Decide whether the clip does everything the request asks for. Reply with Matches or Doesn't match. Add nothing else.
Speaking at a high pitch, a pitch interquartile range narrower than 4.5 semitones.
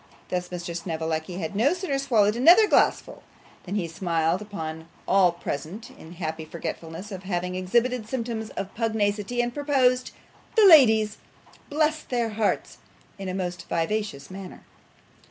Doesn't match